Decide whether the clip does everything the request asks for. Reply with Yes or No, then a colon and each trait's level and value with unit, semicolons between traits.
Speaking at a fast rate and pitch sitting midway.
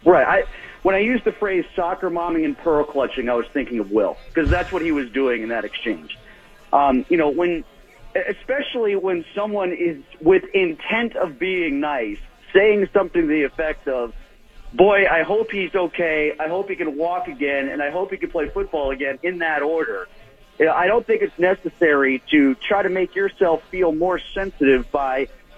No: average, 195 wpm; medium, 180 Hz